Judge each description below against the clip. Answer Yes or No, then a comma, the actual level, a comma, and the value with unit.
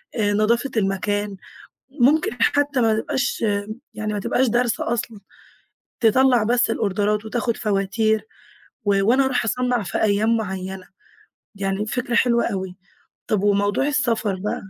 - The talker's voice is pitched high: Yes, high, 220 Hz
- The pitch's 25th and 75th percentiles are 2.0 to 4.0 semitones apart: Yes, average, 3.0 semitones